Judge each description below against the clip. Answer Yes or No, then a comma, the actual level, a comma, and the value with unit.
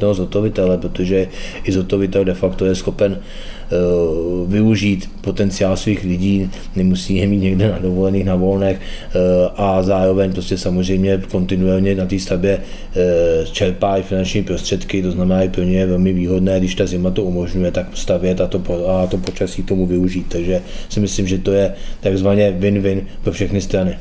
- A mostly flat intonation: Yes, narrow, 1.2 semitones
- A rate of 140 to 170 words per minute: Yes, average, 165 wpm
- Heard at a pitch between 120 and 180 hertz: No, very low, 95 Hz